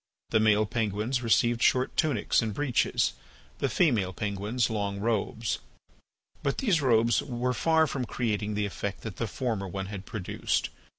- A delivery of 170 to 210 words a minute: No, average, 155 wpm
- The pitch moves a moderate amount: Yes, average, 3.5 semitones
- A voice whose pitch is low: Yes, low, 110 Hz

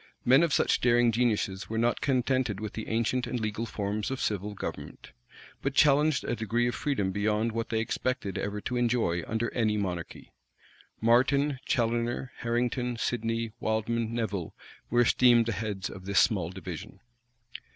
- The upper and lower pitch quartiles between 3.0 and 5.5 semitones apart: No, narrow, 2.6 semitones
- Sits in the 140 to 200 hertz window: No, low, 115 Hz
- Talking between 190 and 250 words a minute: No, average, 160 wpm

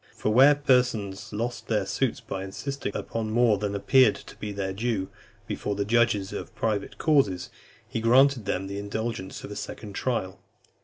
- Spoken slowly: No, average, 170 wpm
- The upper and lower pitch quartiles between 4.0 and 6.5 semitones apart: No, average, 3.5 semitones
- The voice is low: Yes, low, 110 Hz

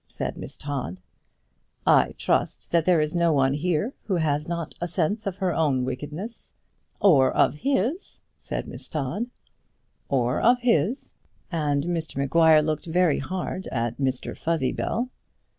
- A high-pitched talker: No, medium, 160 Hz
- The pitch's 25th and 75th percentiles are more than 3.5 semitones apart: Yes, average, 4.5 semitones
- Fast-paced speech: No, average, 145 wpm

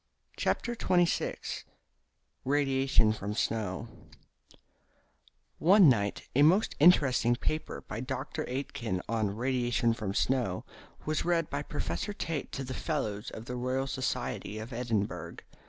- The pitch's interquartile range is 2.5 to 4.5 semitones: No, average, 4.9 semitones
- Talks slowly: Yes, slow, 120 wpm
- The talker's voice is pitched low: Yes, low, 130 Hz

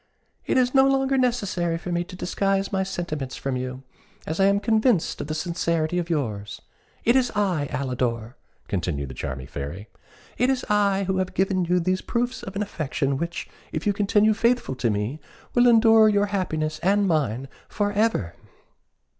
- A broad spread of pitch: Yes, wide, 7.1 semitones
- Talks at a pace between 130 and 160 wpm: No, average, 180 wpm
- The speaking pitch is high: No, medium, 180 Hz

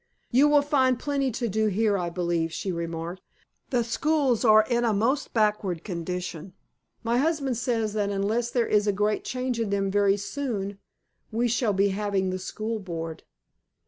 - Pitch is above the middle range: Yes, high, 215 Hz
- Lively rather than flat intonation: No, average, 3.9 semitones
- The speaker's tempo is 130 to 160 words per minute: No, average, 175 wpm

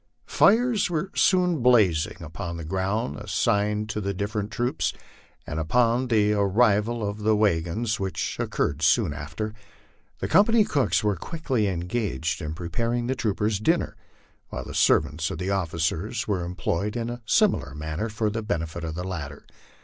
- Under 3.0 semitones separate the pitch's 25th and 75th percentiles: No, wide, 5.6 semitones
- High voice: No, low, 105 Hz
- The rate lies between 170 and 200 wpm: No, average, 160 wpm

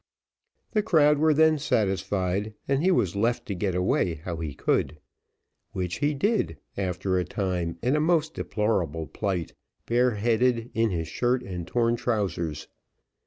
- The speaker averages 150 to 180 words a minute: Yes, average, 155 wpm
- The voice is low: Yes, low, 105 Hz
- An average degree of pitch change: No, wide, 6.0 semitones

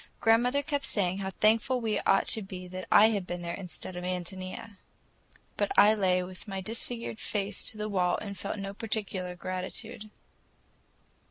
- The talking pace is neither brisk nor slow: Yes, average, 170 wpm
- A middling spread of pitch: Yes, average, 3.0 semitones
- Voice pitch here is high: Yes, high, 200 Hz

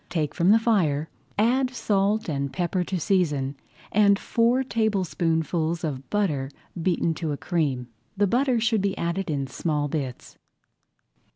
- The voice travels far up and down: Yes, wide, 5.7 semitones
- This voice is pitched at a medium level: Yes, medium, 175 Hz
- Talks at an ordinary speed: Yes, average, 145 wpm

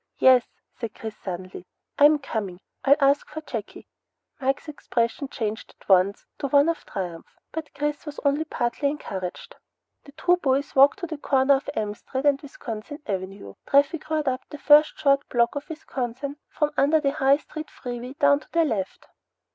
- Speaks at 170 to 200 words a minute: Yes, average, 175 wpm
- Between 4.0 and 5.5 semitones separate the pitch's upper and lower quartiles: Yes, average, 4.3 semitones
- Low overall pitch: No, very high, 275 Hz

